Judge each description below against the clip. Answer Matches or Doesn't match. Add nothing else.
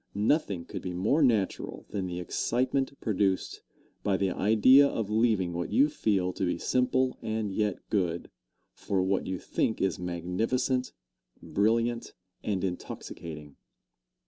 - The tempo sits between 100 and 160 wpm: Matches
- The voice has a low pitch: Matches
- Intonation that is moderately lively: Matches